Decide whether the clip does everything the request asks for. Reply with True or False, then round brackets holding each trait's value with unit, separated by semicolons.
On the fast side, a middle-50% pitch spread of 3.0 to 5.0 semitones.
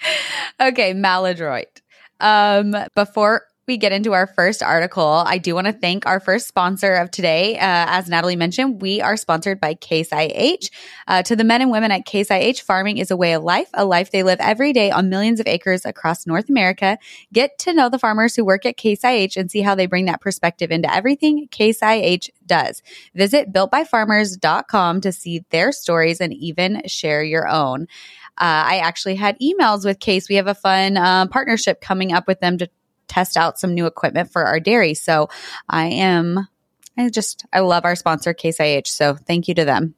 False (195 wpm; 3.5 semitones)